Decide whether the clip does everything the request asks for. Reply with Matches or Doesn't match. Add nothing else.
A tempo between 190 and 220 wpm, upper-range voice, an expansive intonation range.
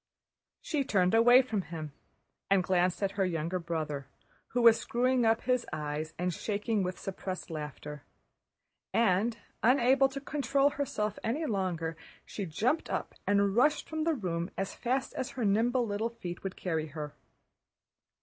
Doesn't match